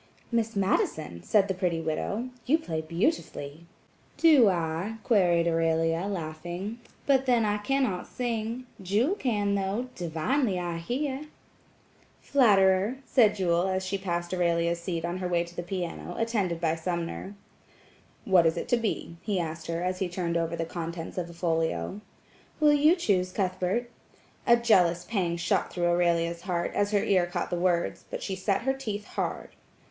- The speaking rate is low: No, average, 165 wpm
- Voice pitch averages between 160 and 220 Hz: Yes, medium, 185 Hz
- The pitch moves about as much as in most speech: Yes, average, 4.2 semitones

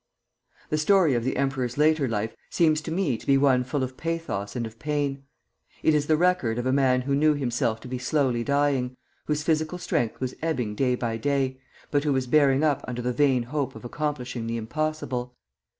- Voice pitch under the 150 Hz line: Yes, low, 135 Hz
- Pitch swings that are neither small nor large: Yes, average, 3.5 semitones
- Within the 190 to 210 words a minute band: Yes, fast, 205 wpm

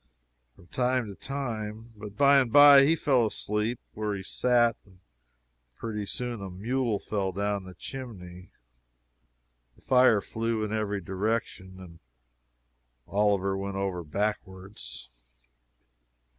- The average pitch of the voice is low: Yes, low, 105 Hz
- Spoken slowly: Yes, slow, 125 wpm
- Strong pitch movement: No, average, 3.6 semitones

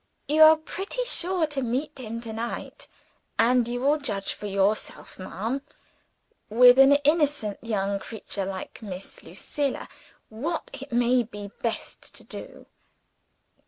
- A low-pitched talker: No, high, 240 Hz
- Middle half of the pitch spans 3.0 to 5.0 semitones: No, wide, 5.4 semitones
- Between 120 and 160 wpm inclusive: Yes, slow, 135 wpm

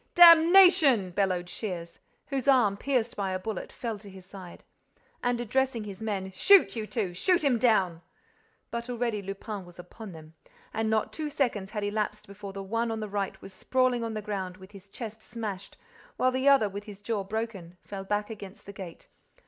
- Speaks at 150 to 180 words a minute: No, average, 190 wpm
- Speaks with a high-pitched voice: Yes, high, 210 Hz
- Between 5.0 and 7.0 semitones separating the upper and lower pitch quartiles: No, average, 3.6 semitones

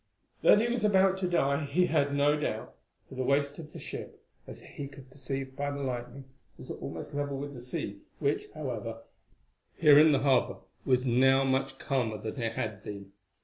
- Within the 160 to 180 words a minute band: No, average, 190 wpm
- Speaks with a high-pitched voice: No, medium, 140 Hz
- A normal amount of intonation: No, narrow, 2.3 semitones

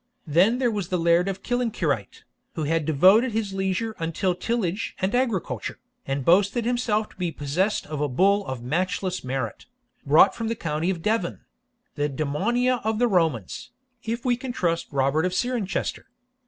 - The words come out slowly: No, average, 170 wpm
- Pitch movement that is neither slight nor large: No, wide, 6.2 semitones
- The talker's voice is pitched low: No, medium, 185 Hz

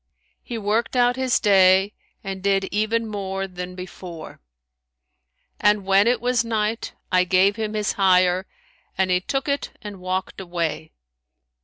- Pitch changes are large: No, average, 3.0 semitones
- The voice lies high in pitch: Yes, high, 195 Hz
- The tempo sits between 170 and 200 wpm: No, average, 145 wpm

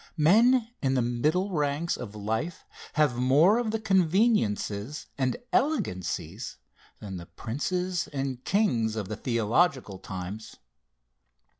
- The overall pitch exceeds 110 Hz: Yes, medium, 140 Hz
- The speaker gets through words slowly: Yes, slow, 120 wpm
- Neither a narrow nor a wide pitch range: No, wide, 8.6 semitones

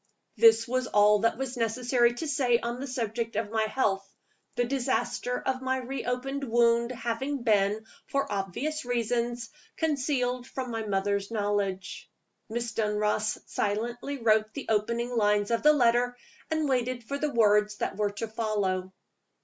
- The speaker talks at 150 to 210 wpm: Yes, average, 155 wpm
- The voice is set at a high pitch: Yes, high, 235 Hz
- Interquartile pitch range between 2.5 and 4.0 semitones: Yes, average, 3.1 semitones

